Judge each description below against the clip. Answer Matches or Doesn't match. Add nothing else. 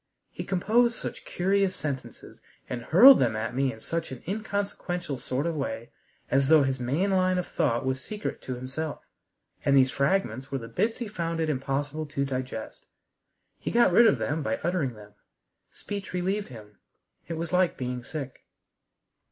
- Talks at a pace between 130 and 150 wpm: Doesn't match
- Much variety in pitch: Matches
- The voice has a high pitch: Doesn't match